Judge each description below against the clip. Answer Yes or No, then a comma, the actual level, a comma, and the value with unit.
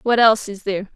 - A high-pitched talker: Yes, high, 210 Hz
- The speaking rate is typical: No, fast, 250 wpm